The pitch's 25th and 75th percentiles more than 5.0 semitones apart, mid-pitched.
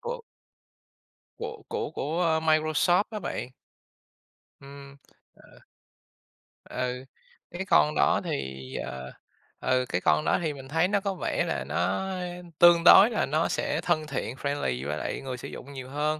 Yes: wide, 5.4 semitones; medium, 150 Hz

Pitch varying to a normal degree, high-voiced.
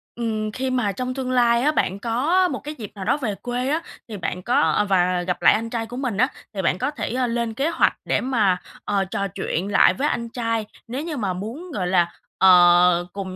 Yes: average, 4.9 semitones; high, 230 Hz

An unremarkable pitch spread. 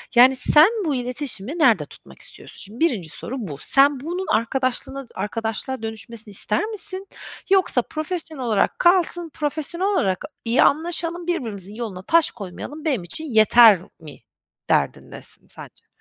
No: wide, 6.9 semitones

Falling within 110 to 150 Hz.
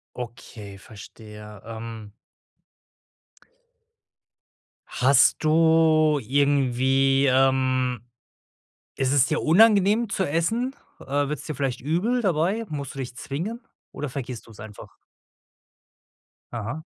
Yes: medium, 140 Hz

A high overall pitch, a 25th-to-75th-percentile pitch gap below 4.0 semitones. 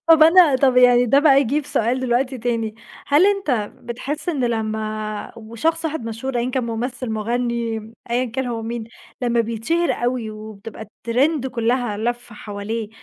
Yes: high, 240 Hz; average, 2.9 semitones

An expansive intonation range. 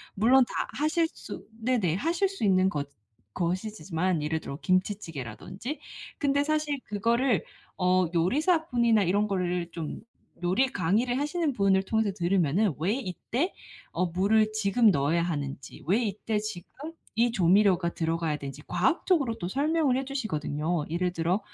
Yes: wide, 6.1 semitones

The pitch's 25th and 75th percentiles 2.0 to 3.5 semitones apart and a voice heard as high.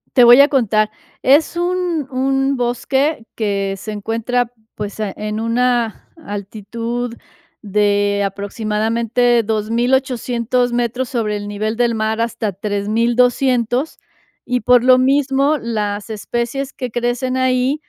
Yes: average, 3.0 semitones; high, 235 Hz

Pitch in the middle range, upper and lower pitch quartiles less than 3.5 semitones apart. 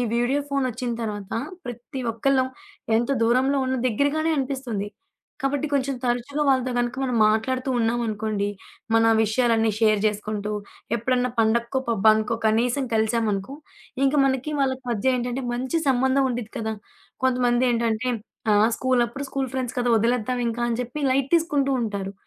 No: high, 245 Hz; average, 2.9 semitones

